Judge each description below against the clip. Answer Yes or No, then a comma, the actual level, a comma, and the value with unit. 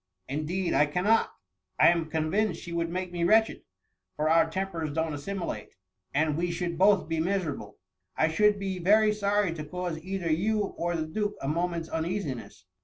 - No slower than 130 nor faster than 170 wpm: No, average, 180 wpm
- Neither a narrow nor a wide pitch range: Yes, average, 3.5 semitones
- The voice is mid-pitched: Yes, medium, 170 Hz